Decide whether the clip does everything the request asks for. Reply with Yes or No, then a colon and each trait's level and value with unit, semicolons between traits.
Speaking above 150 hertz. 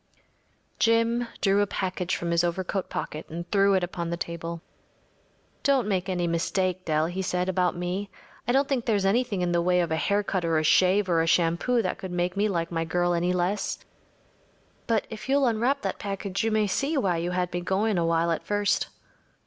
Yes: medium, 185 Hz